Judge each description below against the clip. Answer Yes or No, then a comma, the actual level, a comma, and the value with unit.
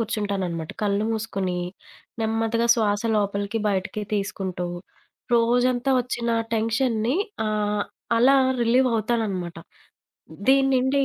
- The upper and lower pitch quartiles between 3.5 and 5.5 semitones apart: No, average, 2.9 semitones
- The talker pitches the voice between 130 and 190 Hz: No, high, 220 Hz